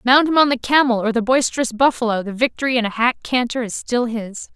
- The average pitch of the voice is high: Yes, high, 240 Hz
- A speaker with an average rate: No, fast, 235 wpm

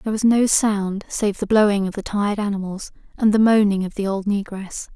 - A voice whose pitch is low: No, high, 205 Hz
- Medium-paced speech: No, fast, 220 wpm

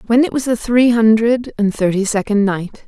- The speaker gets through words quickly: Yes, fast, 210 wpm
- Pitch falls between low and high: No, high, 225 Hz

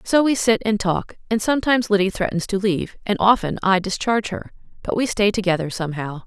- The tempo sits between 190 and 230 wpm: Yes, average, 200 wpm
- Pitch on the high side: Yes, high, 200 Hz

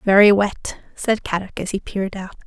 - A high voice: Yes, high, 200 Hz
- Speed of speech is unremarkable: Yes, average, 195 wpm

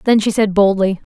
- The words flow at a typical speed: No, fast, 215 wpm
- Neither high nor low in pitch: No, high, 205 Hz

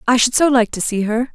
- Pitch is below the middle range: No, high, 240 Hz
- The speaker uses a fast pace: Yes, fast, 310 wpm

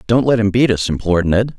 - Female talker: No, male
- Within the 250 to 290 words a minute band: Yes, fast, 265 wpm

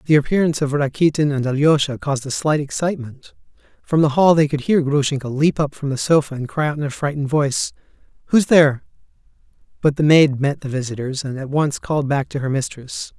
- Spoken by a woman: No, male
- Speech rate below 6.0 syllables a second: No, 6.1 syllables/s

